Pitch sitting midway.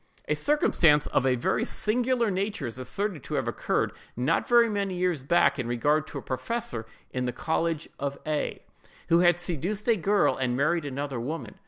Yes: medium, 160 Hz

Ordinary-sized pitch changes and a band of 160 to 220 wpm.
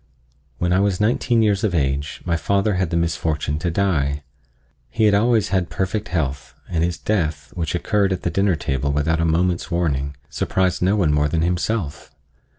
Yes: average, 4.3 semitones; average, 185 wpm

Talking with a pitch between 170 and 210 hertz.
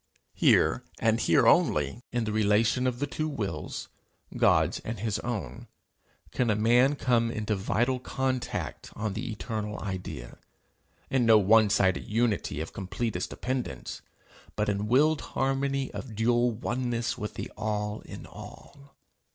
No: low, 115 Hz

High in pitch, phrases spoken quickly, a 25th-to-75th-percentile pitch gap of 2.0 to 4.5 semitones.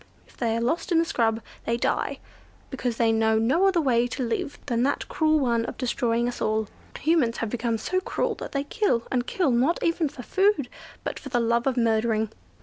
Yes: high, 245 Hz; fast, 215 wpm; average, 4.1 semitones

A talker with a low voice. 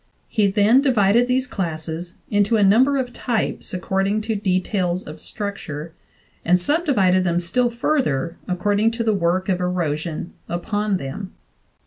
No: high, 195 Hz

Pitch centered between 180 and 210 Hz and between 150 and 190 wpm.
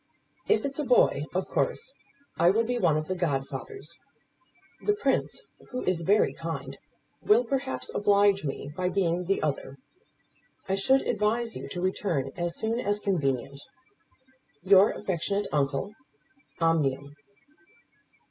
No: high, 190 Hz; slow, 135 wpm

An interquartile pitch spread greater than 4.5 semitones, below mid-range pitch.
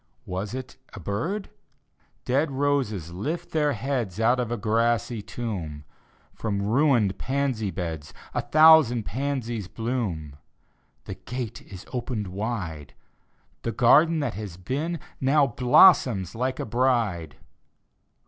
Yes: average, 5.2 semitones; low, 120 Hz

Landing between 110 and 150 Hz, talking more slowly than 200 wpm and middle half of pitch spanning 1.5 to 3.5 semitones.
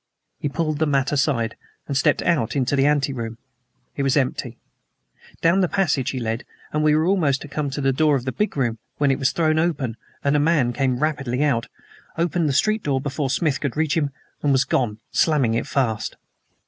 No: medium, 140 Hz; fast, 205 wpm; average, 2.9 semitones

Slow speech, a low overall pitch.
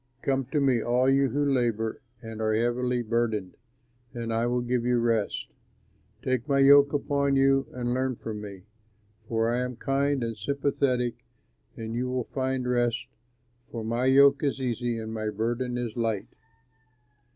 No: average, 160 wpm; low, 125 Hz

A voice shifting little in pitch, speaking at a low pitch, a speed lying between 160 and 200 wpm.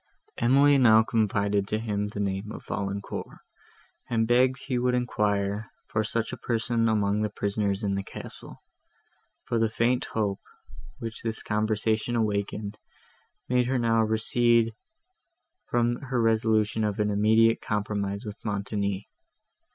No: narrow, 2.2 semitones; low, 110 Hz; slow, 135 wpm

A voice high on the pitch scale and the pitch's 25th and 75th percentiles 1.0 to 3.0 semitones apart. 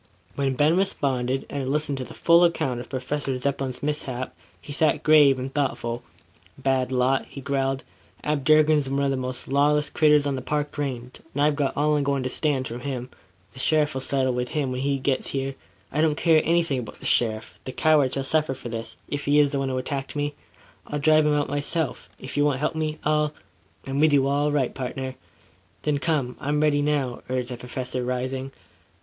No: medium, 140 Hz; narrow, 2.4 semitones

